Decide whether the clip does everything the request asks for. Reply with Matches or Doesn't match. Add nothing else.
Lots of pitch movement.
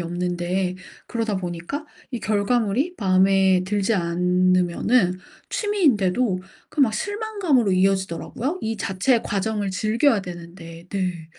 Doesn't match